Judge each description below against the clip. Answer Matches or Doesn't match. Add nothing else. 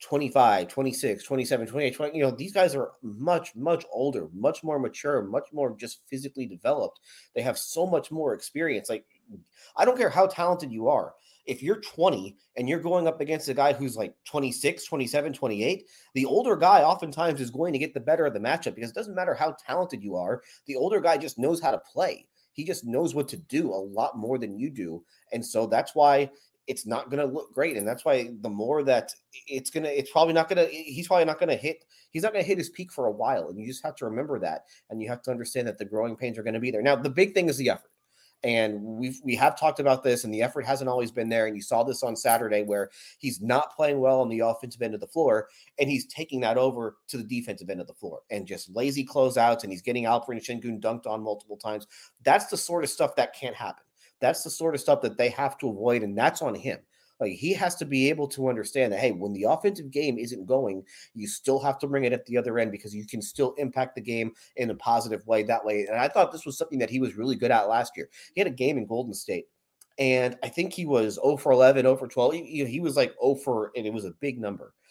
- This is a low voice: Matches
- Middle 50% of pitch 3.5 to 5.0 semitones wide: Matches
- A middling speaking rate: Doesn't match